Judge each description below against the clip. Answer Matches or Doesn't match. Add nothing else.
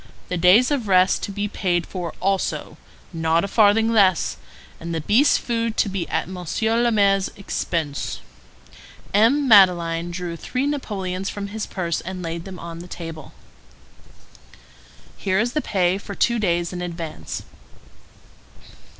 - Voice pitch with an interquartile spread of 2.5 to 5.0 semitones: Matches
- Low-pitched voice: Doesn't match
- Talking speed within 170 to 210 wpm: Doesn't match